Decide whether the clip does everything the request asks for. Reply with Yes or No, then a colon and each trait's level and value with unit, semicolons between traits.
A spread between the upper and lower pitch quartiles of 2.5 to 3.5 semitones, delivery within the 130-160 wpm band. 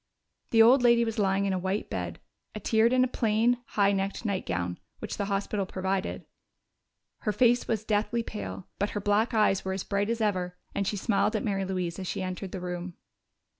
No: average, 2.8 semitones; average, 200 wpm